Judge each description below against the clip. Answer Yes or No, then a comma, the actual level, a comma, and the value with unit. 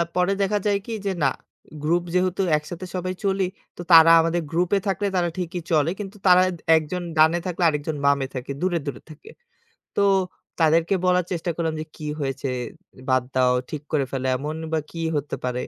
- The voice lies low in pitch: No, medium, 165 Hz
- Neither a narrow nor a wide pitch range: Yes, average, 3.3 semitones